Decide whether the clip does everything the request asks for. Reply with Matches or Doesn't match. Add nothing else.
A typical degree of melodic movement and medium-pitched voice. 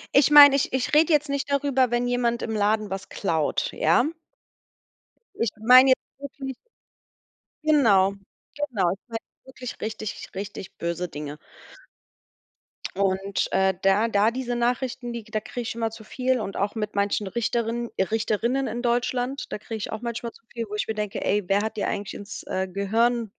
Doesn't match